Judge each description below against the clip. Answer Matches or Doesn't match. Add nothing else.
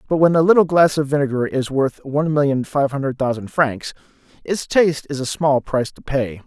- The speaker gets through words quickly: Matches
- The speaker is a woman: Doesn't match